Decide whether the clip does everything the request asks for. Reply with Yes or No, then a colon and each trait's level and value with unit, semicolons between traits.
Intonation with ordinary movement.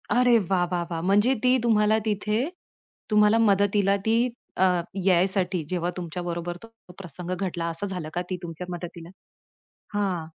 Yes: average, 3.0 semitones